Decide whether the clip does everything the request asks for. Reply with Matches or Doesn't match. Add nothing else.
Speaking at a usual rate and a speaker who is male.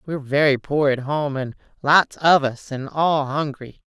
Doesn't match